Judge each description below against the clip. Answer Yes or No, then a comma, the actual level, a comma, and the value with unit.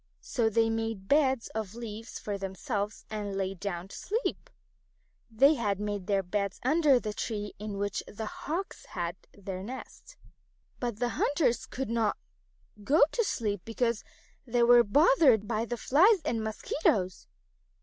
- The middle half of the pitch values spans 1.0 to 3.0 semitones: No, average, 3.9 semitones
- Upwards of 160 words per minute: No, average, 150 wpm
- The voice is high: Yes, high, 225 Hz